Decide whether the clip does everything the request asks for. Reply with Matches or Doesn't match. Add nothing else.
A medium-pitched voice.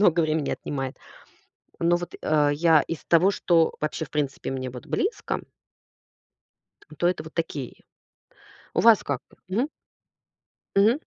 Matches